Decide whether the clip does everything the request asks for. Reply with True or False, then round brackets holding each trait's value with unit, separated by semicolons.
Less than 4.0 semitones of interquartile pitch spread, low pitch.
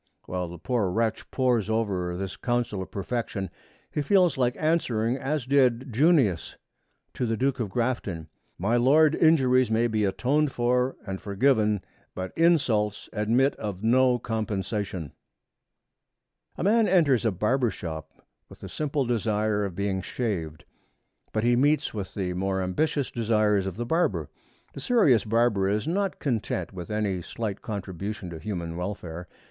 False (5.0 semitones; 110 Hz)